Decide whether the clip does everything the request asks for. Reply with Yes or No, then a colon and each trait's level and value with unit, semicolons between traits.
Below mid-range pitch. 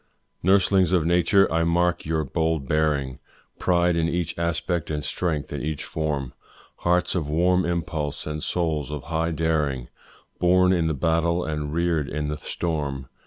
Yes: very low, 80 Hz